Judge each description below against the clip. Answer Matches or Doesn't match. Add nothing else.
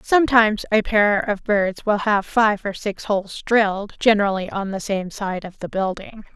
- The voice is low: Doesn't match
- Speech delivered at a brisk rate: Doesn't match